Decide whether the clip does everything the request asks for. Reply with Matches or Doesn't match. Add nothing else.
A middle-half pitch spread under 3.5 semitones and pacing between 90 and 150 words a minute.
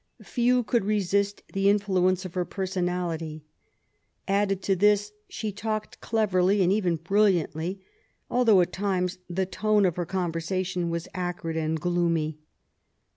Matches